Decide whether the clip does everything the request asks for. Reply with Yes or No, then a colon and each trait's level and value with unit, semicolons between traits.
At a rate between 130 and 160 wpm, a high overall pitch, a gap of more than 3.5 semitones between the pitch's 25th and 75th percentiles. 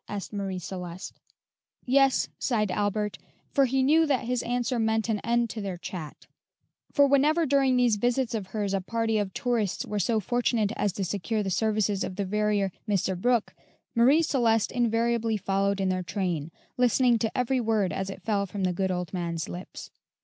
No: average, 185 wpm; high, 215 Hz; average, 3.9 semitones